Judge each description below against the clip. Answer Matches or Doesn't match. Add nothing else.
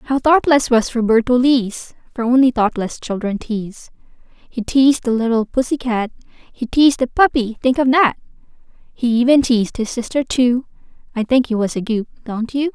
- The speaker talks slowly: Doesn't match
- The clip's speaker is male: Doesn't match